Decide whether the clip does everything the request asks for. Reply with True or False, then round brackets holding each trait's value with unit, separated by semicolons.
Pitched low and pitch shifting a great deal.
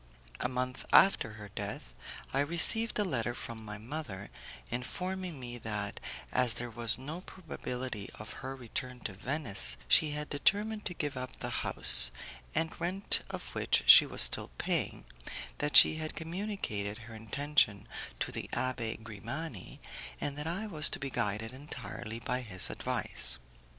True (125 Hz; 6.0 semitones)